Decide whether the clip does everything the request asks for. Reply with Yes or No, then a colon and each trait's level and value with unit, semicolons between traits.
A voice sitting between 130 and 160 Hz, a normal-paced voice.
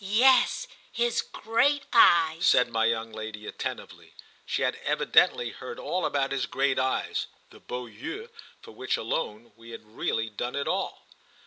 Yes: low, 135 Hz; average, 150 wpm